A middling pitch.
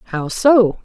No: high, 210 Hz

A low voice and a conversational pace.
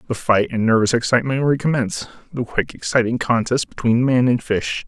Yes: low, 120 Hz; average, 160 wpm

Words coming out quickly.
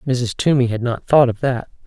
Yes: fast, 225 wpm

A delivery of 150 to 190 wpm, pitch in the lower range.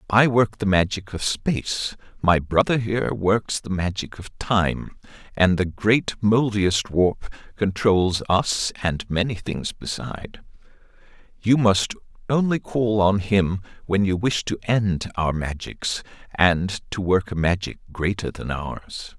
No: average, 140 wpm; low, 100 Hz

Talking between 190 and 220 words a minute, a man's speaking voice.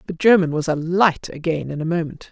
No: fast, 205 wpm; female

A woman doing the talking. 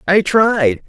No: male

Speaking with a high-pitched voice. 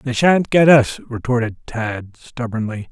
No: low, 120 Hz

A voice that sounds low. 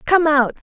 No: very high, 300 Hz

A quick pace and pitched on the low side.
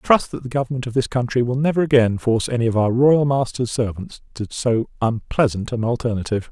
Yes: fast, 210 wpm; low, 120 Hz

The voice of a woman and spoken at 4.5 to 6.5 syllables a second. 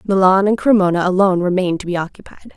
No: female; 6.9 syllables/s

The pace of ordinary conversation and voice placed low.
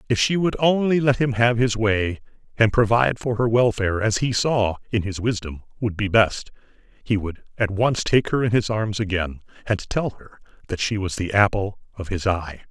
No: fast, 210 wpm; low, 110 Hz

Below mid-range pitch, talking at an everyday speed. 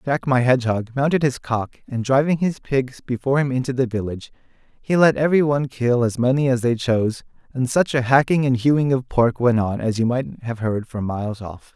No: low, 125 Hz; fast, 220 wpm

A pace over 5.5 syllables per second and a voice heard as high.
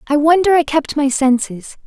No: 4.8 syllables/s; very high, 290 Hz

